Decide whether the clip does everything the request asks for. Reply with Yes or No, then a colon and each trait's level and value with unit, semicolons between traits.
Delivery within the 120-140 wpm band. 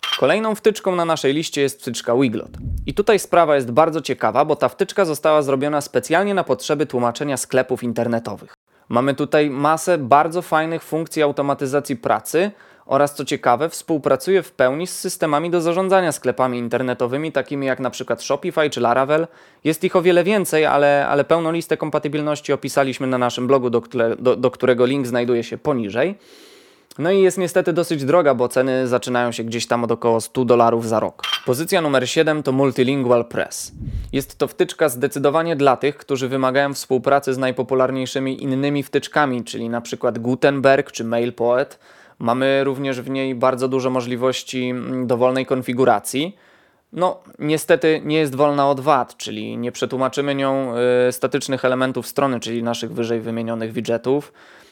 No: fast, 160 wpm